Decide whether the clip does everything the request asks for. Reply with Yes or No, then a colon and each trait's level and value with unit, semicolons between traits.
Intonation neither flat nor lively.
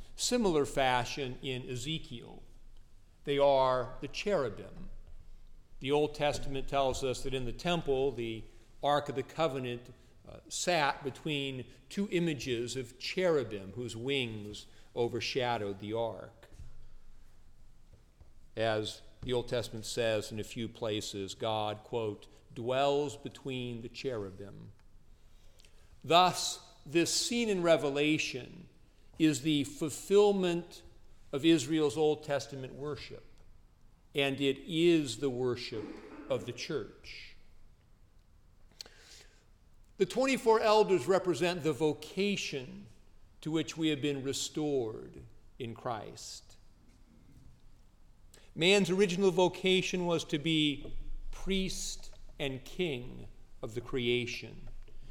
No: wide, 5.9 semitones